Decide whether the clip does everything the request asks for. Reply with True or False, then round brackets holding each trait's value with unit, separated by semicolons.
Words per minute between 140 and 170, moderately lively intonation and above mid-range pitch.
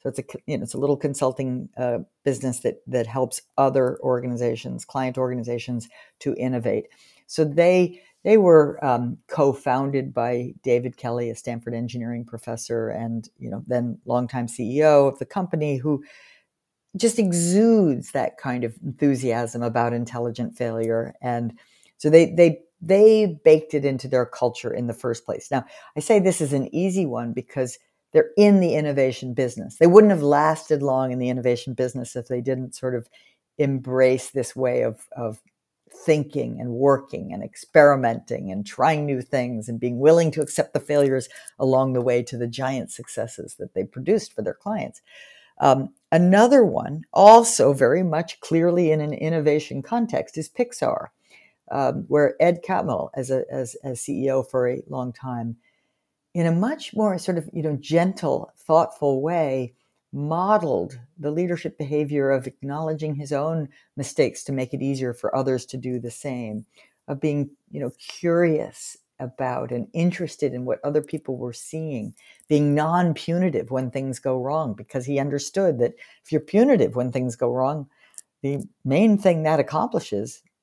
False (165 wpm; 4.3 semitones; 140 Hz)